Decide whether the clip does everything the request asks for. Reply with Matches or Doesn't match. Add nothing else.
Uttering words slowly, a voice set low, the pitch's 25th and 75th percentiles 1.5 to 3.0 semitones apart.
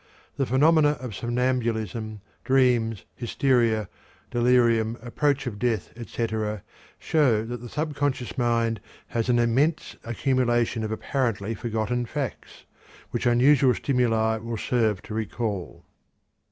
Matches